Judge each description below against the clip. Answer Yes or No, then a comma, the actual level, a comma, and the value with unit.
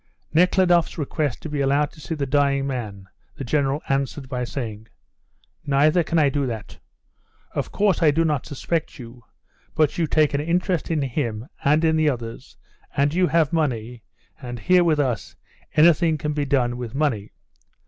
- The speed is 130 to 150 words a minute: No, average, 175 wpm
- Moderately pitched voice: Yes, medium, 145 Hz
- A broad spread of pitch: No, average, 3.9 semitones